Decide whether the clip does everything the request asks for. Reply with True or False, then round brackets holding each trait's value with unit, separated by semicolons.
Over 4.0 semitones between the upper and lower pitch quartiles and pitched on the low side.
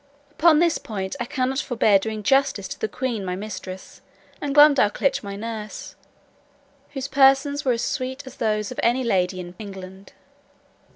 False (5.2 semitones; 230 Hz)